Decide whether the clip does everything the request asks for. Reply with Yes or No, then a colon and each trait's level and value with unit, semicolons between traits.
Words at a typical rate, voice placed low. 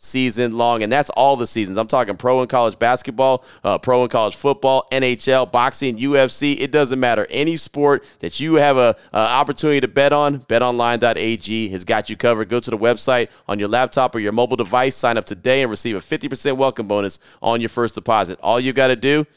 No: fast, 215 wpm; low, 125 Hz